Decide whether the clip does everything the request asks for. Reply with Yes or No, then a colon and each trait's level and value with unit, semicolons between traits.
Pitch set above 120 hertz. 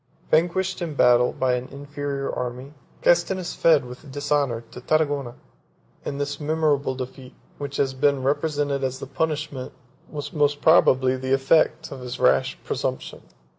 Yes: medium, 140 Hz